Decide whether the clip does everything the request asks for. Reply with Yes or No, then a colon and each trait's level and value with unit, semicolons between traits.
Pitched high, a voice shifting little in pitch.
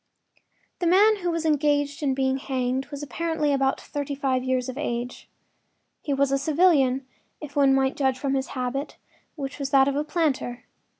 Yes: very high, 275 Hz; narrow, 2.0 semitones